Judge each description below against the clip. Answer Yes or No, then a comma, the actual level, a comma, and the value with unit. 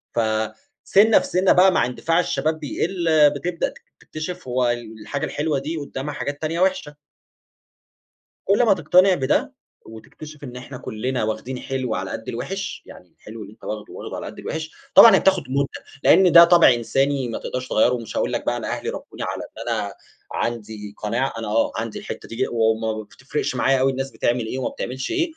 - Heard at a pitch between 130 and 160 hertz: Yes, low, 135 Hz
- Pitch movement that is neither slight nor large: No, wide, 5.7 semitones